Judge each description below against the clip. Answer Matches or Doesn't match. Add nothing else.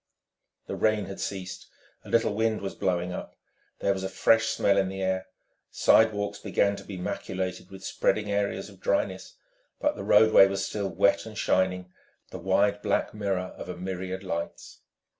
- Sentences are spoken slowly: Doesn't match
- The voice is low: Matches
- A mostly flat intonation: Matches